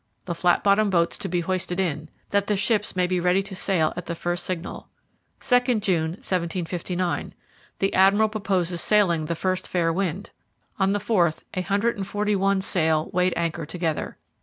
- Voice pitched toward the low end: No, medium, 185 Hz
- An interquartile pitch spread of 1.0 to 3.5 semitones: Yes, narrow, 2.6 semitones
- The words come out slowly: No, average, 180 wpm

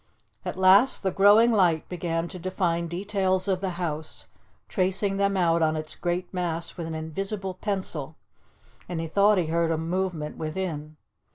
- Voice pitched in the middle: Yes, medium, 180 Hz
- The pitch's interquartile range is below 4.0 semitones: Yes, average, 2.8 semitones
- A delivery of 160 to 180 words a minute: Yes, average, 165 wpm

